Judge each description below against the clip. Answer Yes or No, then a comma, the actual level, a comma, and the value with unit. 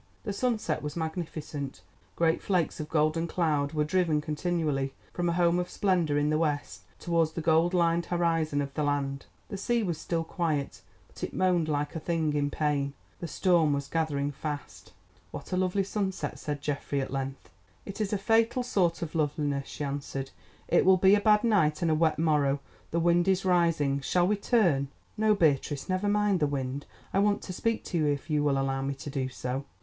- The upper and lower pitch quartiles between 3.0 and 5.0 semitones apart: Yes, average, 3.9 semitones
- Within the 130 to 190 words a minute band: No, average, 200 wpm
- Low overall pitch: No, medium, 160 Hz